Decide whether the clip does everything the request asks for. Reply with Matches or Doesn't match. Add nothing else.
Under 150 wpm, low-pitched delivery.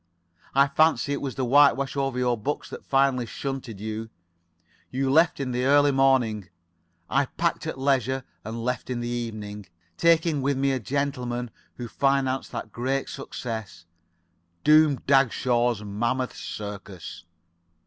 Matches